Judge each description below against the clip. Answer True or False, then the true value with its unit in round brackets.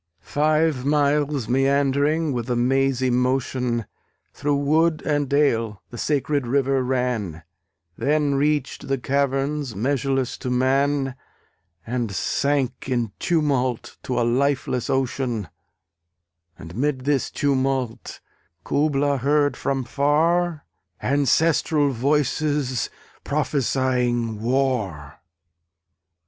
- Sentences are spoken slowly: True (95 wpm)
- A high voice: False (135 Hz)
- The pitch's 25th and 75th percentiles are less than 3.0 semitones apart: True (2.6 semitones)